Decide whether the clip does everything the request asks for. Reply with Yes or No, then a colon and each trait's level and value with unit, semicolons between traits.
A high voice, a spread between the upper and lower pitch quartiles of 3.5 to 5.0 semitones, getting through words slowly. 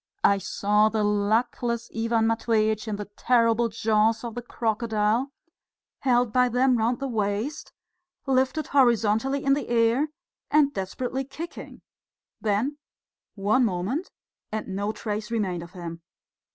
No: high, 225 Hz; average, 3.1 semitones; slow, 130 wpm